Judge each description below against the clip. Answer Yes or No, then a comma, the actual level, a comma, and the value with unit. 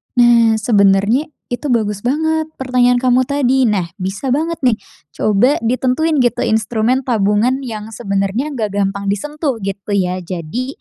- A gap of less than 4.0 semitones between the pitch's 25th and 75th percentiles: No, average, 4.5 semitones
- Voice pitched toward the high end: Yes, high, 235 Hz